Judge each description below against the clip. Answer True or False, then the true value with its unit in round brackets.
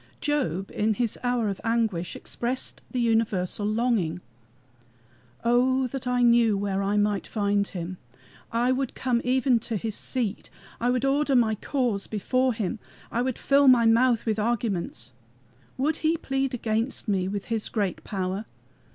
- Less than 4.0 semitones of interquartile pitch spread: True (3.6 semitones)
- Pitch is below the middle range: False (230 Hz)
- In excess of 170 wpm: False (155 wpm)